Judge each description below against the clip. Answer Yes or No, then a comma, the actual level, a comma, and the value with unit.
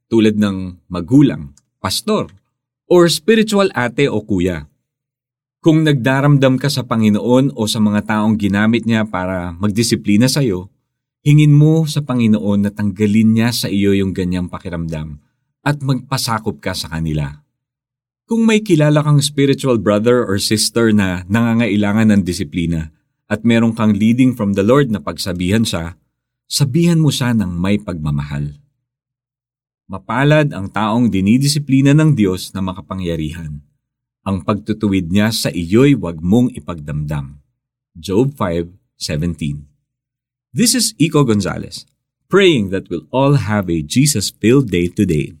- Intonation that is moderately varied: No, wide, 5.8 semitones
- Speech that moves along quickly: No, average, 135 wpm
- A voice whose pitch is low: Yes, low, 110 Hz